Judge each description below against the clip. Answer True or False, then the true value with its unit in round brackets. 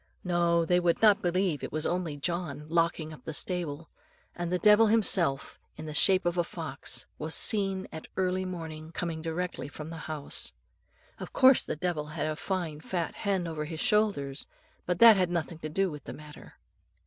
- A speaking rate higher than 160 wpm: True (190 wpm)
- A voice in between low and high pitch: True (170 Hz)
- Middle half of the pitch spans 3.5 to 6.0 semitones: False (3.0 semitones)